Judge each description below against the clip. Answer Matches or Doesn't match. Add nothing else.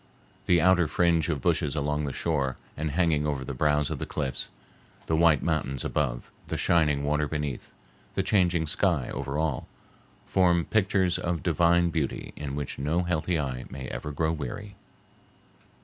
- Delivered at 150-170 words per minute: Matches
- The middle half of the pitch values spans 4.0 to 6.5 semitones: Doesn't match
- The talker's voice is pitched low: Matches